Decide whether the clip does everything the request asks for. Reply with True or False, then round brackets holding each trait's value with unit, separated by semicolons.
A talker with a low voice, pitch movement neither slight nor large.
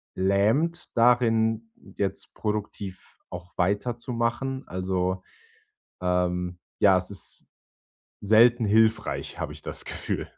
True (105 Hz; 4.0 semitones)